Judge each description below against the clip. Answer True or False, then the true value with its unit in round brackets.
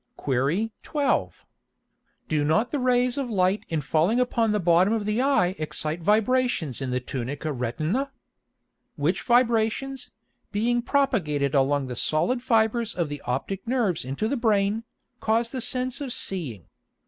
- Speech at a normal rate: True (150 wpm)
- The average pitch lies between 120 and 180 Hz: False (210 Hz)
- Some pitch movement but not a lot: False (8.0 semitones)